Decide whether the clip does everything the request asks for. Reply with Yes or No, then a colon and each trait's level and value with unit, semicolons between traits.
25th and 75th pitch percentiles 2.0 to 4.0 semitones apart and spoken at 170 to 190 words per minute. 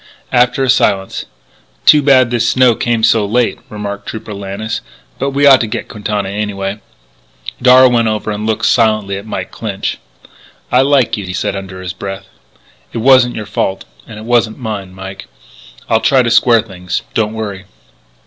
Yes: average, 3.4 semitones; average, 175 wpm